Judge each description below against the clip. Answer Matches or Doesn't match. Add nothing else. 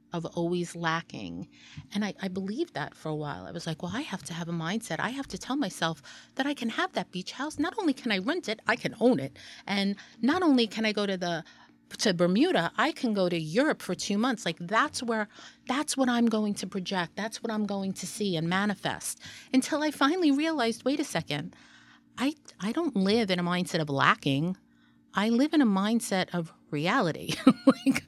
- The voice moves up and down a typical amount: Doesn't match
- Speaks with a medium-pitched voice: Doesn't match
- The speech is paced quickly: Matches